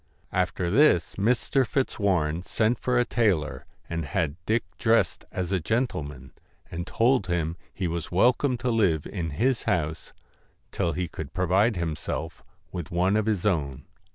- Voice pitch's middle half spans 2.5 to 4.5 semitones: No, wide, 5.5 semitones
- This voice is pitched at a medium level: No, very low, 90 Hz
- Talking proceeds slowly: No, average, 155 wpm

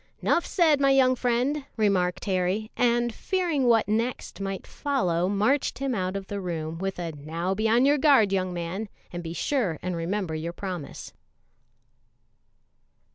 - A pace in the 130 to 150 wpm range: No, average, 160 wpm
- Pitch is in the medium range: No, high, 200 Hz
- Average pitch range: No, wide, 6.1 semitones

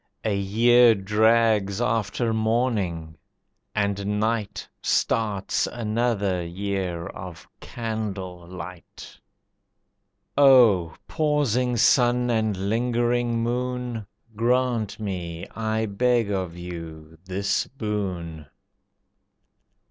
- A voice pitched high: No, low, 105 Hz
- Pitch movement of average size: Yes, average, 4.0 semitones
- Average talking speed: No, slow, 80 wpm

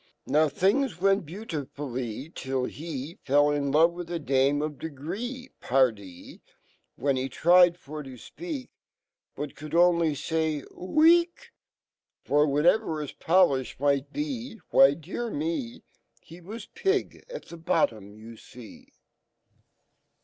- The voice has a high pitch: No, medium, 155 Hz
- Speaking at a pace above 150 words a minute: No, slow, 135 wpm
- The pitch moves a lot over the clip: Yes, wide, 5.9 semitones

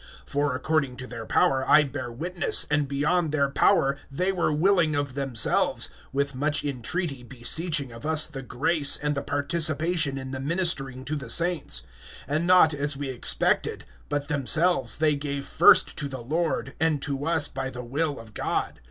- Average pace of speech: Yes, average, 175 wpm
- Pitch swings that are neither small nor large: Yes, average, 3.0 semitones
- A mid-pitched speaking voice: Yes, medium, 145 Hz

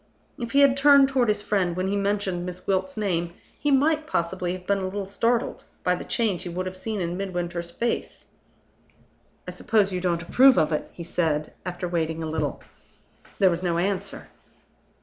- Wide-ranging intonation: No, average, 3.4 semitones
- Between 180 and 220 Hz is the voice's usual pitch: Yes, medium, 185 Hz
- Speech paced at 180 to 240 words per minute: Yes, average, 190 wpm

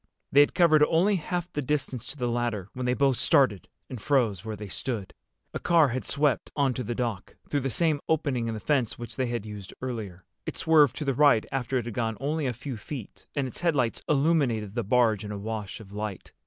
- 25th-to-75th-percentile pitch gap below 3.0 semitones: No, average, 4.6 semitones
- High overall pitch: No, low, 125 Hz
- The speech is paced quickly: Yes, fast, 225 wpm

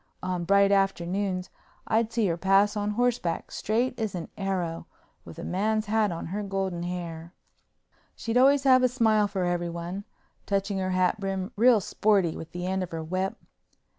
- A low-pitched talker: No, high, 195 Hz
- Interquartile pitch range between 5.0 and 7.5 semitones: No, average, 3.3 semitones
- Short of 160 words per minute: No, average, 170 wpm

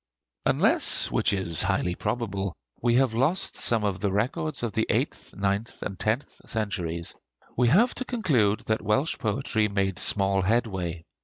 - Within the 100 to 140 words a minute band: No, average, 155 wpm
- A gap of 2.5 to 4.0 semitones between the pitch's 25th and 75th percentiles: Yes, average, 3.6 semitones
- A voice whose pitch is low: Yes, low, 105 Hz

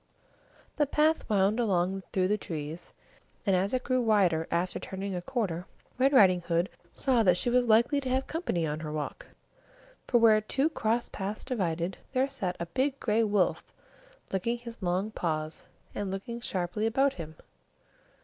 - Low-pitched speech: No, high, 205 Hz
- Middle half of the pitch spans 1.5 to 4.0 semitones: No, wide, 5.4 semitones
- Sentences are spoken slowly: No, average, 165 wpm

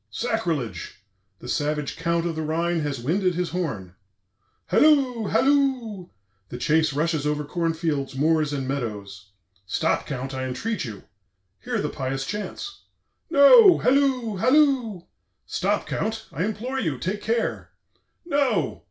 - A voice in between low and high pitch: Yes, medium, 170 Hz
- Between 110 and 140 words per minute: Yes, slow, 135 wpm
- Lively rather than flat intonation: Yes, wide, 8.2 semitones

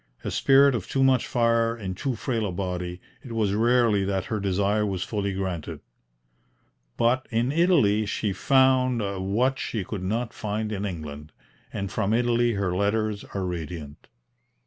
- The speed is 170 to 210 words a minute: No, average, 160 wpm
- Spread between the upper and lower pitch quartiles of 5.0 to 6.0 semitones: No, average, 3.8 semitones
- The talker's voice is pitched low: Yes, low, 105 Hz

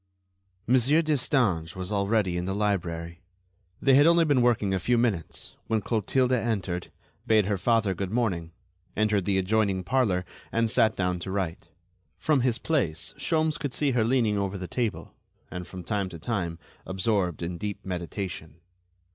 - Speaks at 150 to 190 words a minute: Yes, average, 165 wpm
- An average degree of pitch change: Yes, average, 4.7 semitones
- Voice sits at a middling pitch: No, low, 100 Hz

